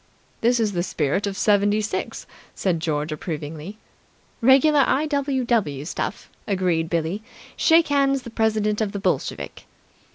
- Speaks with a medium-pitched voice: No, high, 205 Hz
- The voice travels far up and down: Yes, wide, 6.8 semitones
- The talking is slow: Yes, slow, 125 wpm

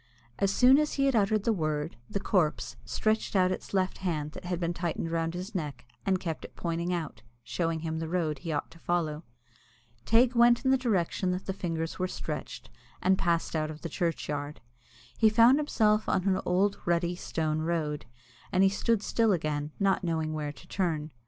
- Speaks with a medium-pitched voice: Yes, medium, 175 Hz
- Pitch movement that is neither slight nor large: Yes, average, 3.8 semitones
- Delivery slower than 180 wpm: No, average, 200 wpm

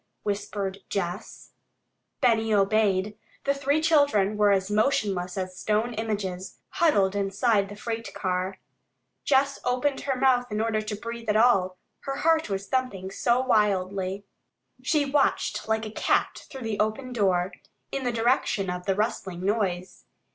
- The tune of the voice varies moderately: Yes, average, 4.2 semitones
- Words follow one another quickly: No, average, 145 wpm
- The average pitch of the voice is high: Yes, high, 215 Hz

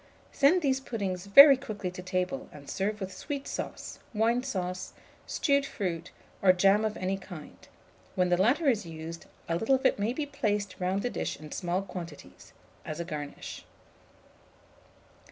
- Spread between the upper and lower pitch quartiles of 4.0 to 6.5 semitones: Yes, average, 5.2 semitones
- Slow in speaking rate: No, average, 165 wpm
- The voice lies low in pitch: No, high, 195 Hz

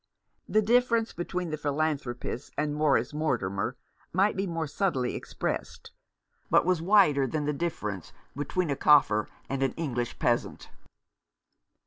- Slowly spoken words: Yes, slow, 130 wpm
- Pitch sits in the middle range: Yes, medium, 150 Hz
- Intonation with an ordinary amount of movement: Yes, average, 4.9 semitones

